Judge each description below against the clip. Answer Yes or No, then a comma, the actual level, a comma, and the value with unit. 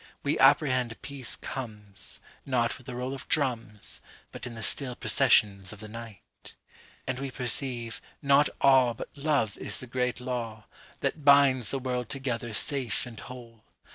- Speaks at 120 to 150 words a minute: Yes, average, 140 wpm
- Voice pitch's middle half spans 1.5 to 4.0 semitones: Yes, average, 2.8 semitones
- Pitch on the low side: Yes, low, 125 Hz